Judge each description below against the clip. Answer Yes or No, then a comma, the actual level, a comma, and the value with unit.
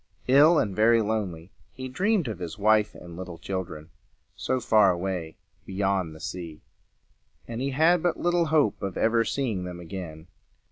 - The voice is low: Yes, low, 105 Hz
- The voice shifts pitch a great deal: Yes, wide, 6.6 semitones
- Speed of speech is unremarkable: Yes, average, 160 wpm